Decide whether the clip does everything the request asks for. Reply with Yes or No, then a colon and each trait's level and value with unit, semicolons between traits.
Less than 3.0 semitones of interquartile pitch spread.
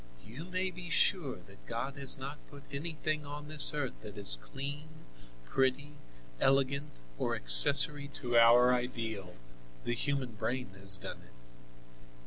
No: average, 4.3 semitones